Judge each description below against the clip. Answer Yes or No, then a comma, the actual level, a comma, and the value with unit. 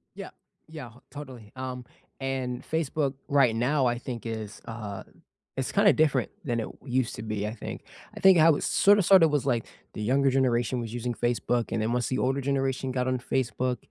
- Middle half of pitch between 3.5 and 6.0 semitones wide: No, average, 2.7 semitones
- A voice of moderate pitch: No, low, 130 Hz